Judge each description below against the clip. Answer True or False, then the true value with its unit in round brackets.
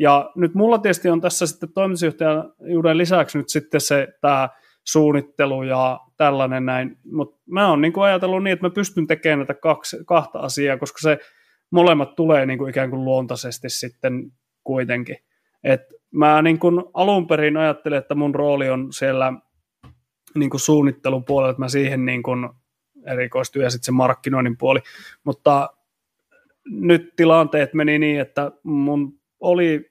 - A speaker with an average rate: True (145 wpm)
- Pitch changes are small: False (3.6 semitones)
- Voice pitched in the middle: True (145 Hz)